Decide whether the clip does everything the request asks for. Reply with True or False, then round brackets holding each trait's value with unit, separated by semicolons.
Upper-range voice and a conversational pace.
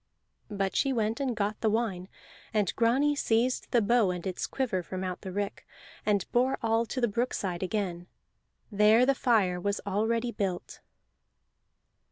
True (215 Hz; 160 wpm)